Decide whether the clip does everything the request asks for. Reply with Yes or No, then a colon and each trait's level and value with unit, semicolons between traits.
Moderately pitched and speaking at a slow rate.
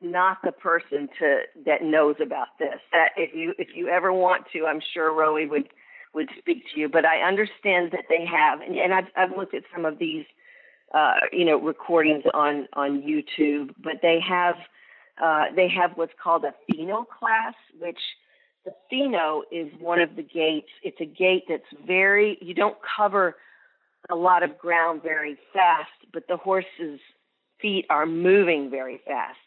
No: medium, 170 Hz; average, 175 wpm